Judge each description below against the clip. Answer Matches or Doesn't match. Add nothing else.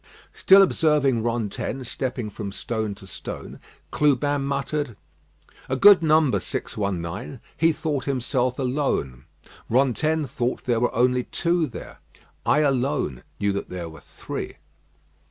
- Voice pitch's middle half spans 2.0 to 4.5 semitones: Doesn't match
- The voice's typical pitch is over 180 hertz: Doesn't match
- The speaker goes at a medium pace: Doesn't match